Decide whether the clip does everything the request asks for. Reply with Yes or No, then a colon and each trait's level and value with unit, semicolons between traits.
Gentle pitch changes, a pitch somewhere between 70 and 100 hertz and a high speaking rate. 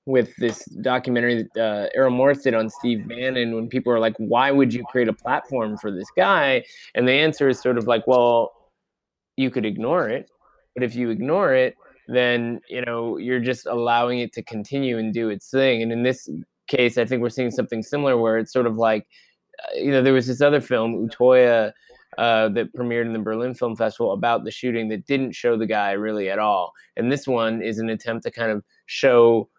No: narrow, 2.1 semitones; low, 120 Hz; fast, 215 wpm